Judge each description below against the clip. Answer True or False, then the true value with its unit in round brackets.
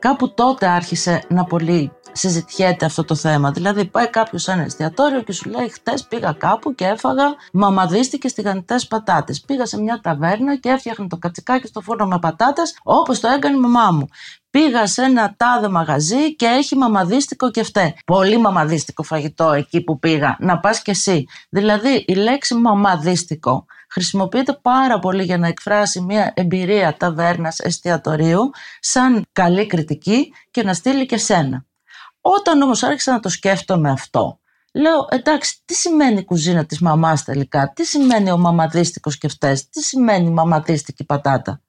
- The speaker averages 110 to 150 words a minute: False (160 wpm)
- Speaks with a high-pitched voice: True (195 Hz)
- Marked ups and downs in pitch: True (6.8 semitones)